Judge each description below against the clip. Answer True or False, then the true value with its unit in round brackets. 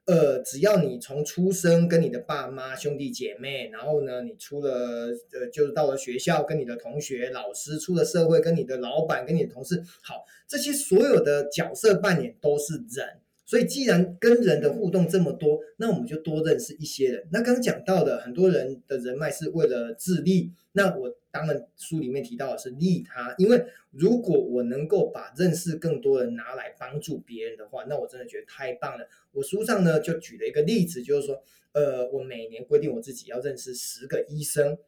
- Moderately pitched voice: True (155 Hz)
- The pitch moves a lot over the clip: True (6.3 semitones)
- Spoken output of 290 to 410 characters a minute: True (300 characters per minute)